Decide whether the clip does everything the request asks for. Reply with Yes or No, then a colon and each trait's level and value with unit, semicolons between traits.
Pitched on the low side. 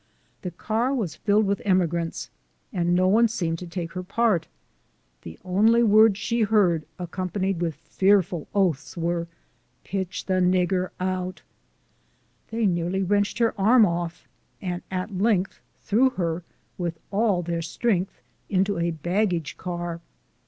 No: medium, 185 Hz